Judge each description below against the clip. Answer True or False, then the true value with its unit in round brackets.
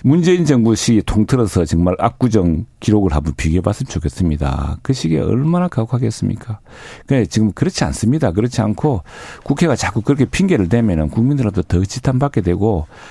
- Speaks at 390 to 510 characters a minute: True (405 characters per minute)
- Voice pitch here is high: False (110 Hz)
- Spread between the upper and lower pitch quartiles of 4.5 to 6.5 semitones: True (5.8 semitones)